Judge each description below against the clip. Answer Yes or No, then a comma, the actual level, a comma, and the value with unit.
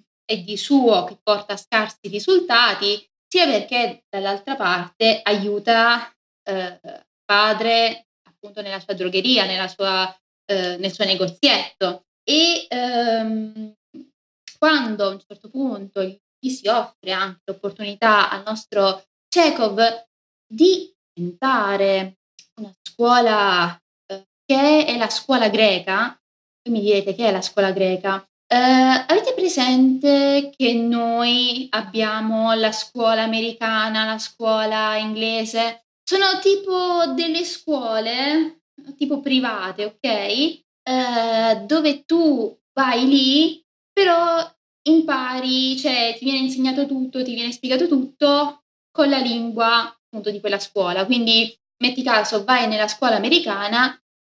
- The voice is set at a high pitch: Yes, high, 230 Hz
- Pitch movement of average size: Yes, average, 4.6 semitones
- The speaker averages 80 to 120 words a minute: Yes, slow, 115 wpm